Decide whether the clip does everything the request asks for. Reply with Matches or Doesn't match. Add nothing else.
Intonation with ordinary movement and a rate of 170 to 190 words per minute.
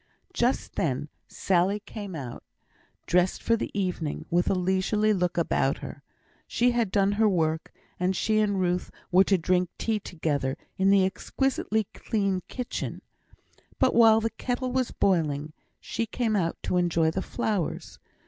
Doesn't match